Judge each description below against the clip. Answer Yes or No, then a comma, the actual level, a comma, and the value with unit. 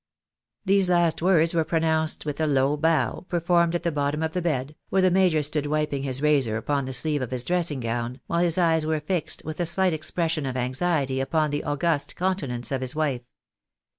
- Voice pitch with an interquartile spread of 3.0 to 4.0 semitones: Yes, average, 3.7 semitones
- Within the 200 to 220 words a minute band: Yes, fast, 205 wpm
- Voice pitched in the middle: Yes, medium, 155 Hz